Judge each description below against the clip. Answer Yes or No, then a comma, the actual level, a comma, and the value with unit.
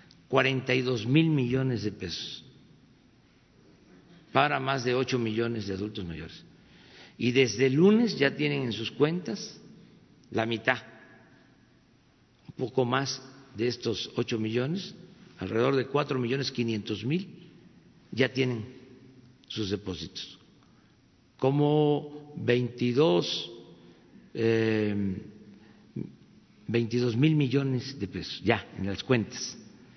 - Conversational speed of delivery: No, slow, 110 wpm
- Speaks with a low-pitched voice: Yes, low, 125 Hz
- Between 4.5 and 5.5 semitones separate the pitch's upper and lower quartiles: No, average, 3.3 semitones